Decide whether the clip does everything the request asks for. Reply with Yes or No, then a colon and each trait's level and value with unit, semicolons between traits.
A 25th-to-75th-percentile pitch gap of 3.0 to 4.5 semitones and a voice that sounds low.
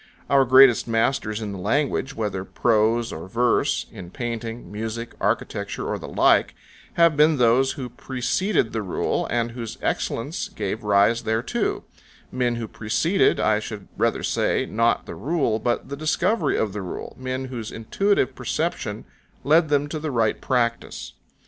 Yes: average, 3.6 semitones; low, 120 Hz